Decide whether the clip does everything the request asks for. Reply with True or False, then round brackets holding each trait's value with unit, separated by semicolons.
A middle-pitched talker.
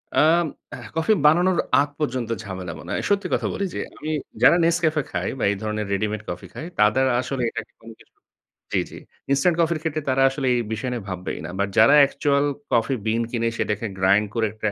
False (130 Hz)